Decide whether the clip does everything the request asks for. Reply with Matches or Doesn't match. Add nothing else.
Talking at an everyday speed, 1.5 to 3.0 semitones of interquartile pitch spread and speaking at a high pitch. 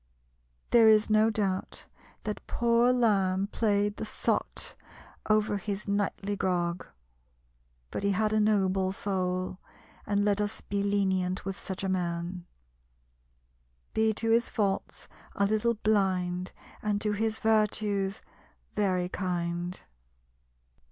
Doesn't match